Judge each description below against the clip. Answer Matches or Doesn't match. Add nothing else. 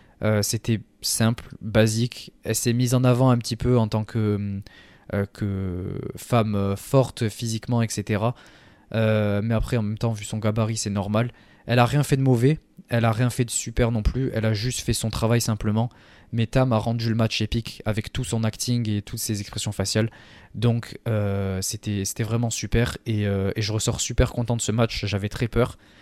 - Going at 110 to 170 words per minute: Doesn't match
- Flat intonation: Matches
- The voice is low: Matches